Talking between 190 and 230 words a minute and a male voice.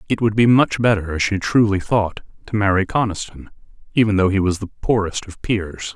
Yes: average, 200 wpm; male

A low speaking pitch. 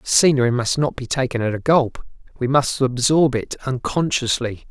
Yes: low, 130 Hz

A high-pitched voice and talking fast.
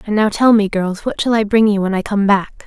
Yes: high, 210 Hz; fast, 315 wpm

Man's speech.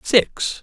Yes: male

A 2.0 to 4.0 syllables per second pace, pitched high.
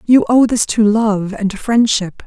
Yes: 3.8 syllables/s; high, 215 Hz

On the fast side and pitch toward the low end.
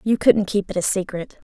No: fast, 235 wpm; high, 200 Hz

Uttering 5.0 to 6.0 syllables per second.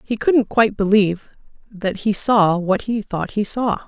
No: 4.5 syllables/s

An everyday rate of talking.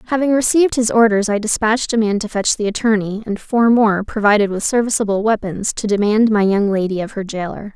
No: fast, 210 wpm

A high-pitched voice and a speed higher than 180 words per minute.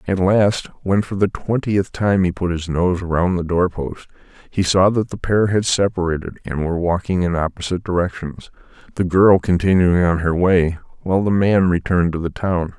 No: very low, 90 Hz; average, 190 wpm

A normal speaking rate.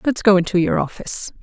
No: fast, 210 wpm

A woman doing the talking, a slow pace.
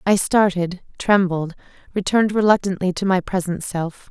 Yes: female; slow, 130 wpm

